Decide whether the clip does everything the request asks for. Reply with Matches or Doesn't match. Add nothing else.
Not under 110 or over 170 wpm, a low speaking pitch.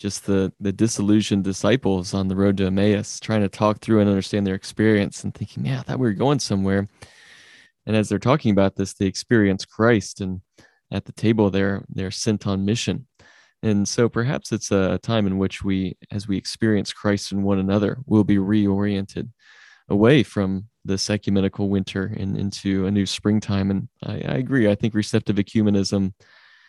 Doesn't match